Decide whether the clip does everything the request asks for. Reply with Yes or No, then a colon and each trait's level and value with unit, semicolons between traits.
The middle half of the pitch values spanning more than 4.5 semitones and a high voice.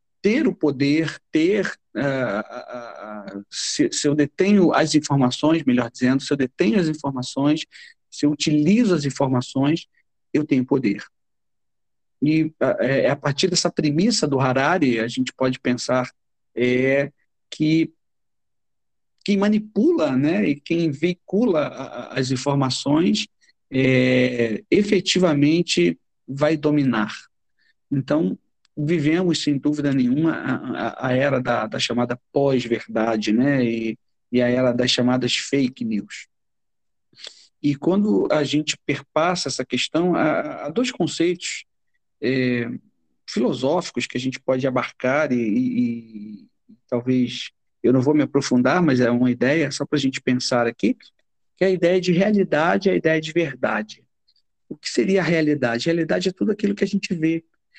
No: average, 5.1 semitones; medium, 145 Hz